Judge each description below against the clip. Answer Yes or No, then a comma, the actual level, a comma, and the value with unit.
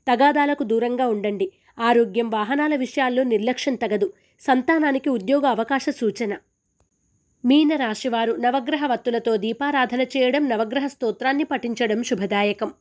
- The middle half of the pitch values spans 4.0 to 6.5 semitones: No, average, 3.5 semitones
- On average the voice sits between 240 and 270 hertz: Yes, high, 245 Hz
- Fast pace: No, average, 100 wpm